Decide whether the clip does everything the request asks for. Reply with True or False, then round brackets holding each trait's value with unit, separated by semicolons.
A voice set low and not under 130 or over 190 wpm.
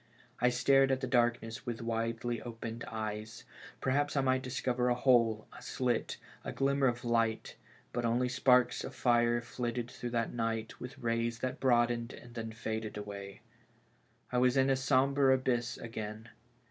True (120 Hz; 160 wpm)